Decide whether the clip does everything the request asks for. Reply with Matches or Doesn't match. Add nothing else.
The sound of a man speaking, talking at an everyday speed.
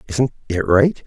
Matches